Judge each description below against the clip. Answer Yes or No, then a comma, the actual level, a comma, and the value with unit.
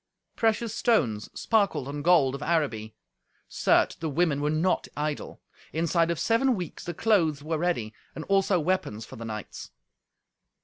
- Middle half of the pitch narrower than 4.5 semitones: No, average, 4.8 semitones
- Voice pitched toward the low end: No, medium, 160 Hz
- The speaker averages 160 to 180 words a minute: No, average, 150 wpm